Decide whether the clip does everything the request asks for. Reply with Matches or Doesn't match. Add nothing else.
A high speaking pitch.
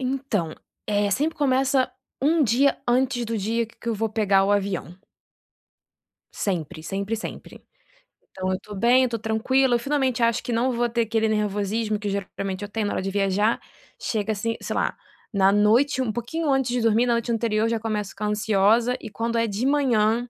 Matches